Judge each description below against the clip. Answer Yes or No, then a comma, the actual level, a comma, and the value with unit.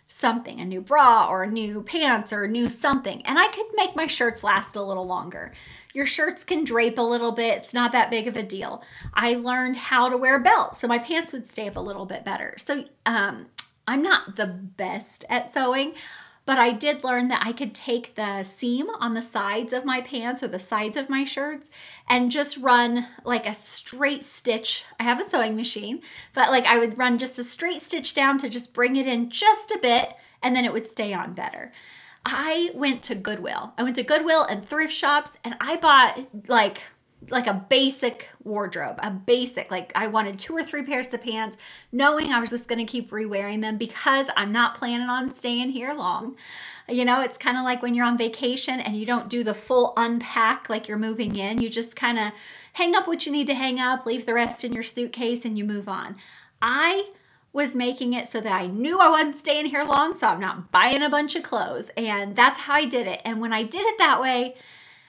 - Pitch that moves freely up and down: No, average, 3.8 semitones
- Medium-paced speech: No, fast, 225 wpm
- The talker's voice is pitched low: No, high, 245 Hz